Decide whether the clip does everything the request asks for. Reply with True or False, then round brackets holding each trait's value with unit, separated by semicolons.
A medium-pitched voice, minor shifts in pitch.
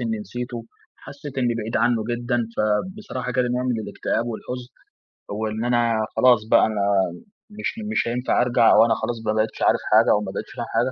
False (120 Hz; 2.1 semitones)